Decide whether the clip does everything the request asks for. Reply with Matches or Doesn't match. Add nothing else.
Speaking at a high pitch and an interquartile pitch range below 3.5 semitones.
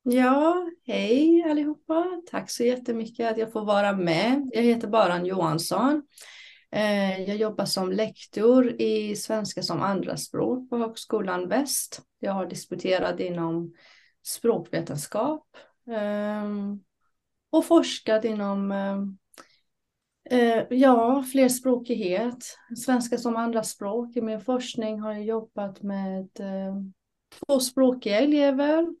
Doesn't match